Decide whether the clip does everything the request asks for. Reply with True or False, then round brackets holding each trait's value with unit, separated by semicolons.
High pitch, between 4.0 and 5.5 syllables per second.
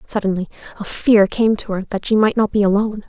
False (205 Hz; 6.1 syllables/s)